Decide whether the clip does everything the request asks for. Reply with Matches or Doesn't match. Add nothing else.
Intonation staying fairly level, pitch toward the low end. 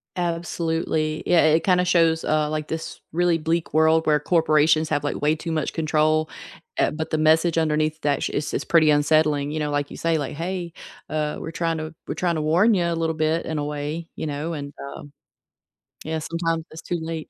Doesn't match